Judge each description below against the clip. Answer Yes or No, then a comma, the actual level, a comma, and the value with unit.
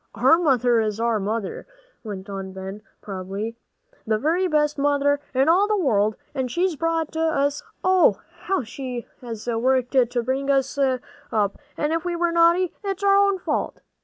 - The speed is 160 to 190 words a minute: Yes, average, 170 wpm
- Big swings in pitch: Yes, wide, 6.6 semitones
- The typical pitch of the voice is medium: No, very high, 270 Hz